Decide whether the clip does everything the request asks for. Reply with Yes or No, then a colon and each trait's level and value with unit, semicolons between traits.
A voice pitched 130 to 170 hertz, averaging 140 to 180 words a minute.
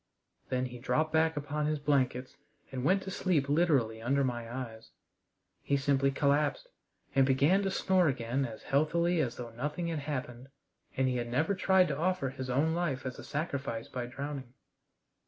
Yes: medium, 140 Hz; average, 175 wpm